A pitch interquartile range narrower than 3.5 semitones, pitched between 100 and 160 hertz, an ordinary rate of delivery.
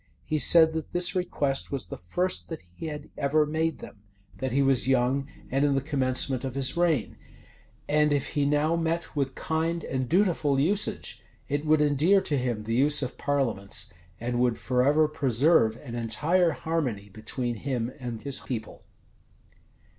No: average, 4.1 semitones; medium, 140 Hz; average, 170 wpm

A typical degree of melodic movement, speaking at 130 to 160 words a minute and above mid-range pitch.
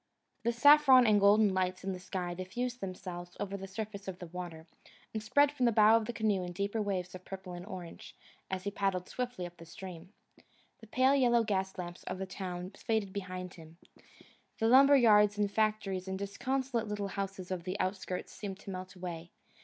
No: average, 3.1 semitones; average, 195 wpm; high, 195 Hz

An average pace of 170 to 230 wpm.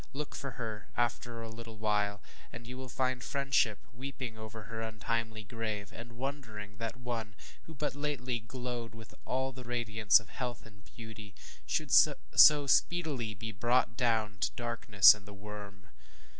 No: average, 155 wpm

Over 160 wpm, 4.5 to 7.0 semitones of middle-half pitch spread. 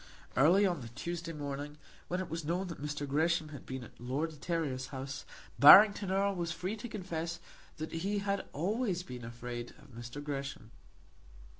Yes: average, 175 wpm; average, 4.9 semitones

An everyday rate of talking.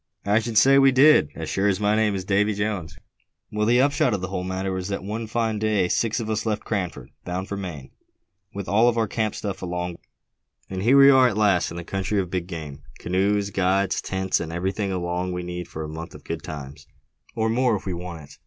No: fast, 230 wpm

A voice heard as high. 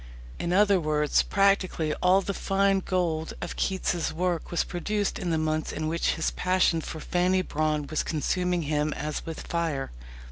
No: medium, 170 Hz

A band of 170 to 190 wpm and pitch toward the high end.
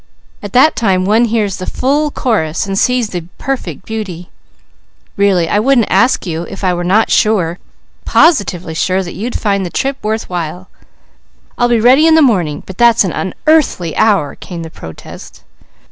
Yes: average, 175 wpm; high, 200 Hz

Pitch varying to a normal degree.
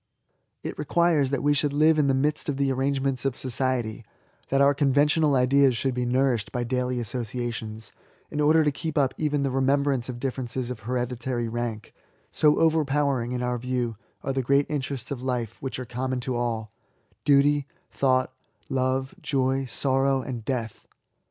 No: narrow, 2.3 semitones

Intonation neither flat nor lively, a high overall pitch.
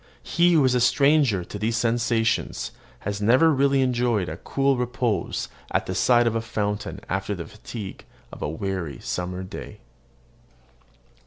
No: average, 4.1 semitones; low, 115 Hz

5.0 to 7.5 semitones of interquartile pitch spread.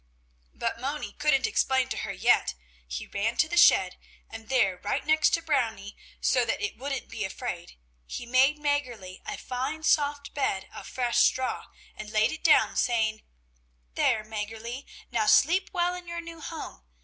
Yes: wide, 5.5 semitones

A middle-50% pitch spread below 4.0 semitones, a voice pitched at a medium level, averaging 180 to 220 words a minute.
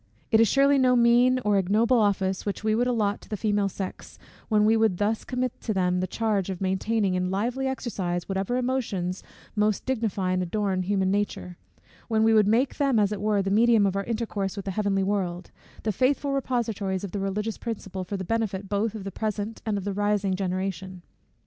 No: average, 2.8 semitones; high, 205 Hz; fast, 205 wpm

